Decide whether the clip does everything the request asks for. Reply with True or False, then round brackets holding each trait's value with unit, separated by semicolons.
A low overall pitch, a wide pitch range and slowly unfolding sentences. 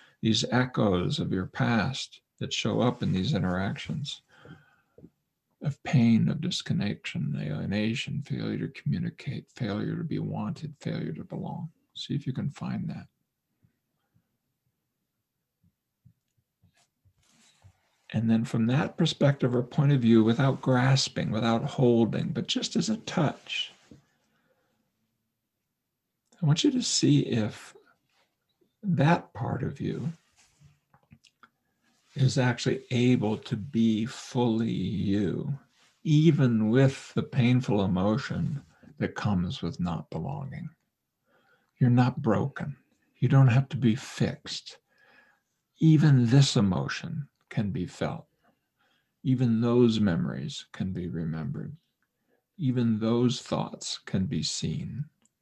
False (130 Hz; 4.7 semitones; 115 wpm)